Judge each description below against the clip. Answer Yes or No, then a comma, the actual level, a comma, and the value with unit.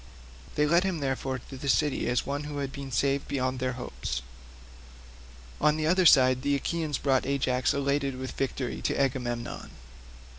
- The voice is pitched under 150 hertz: Yes, low, 135 Hz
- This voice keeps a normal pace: Yes, average, 170 wpm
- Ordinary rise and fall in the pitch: No, narrow, 2.1 semitones